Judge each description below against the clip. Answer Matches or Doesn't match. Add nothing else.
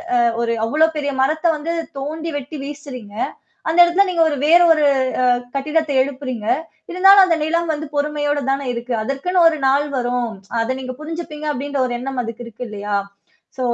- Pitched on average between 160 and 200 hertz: Doesn't match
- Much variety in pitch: Doesn't match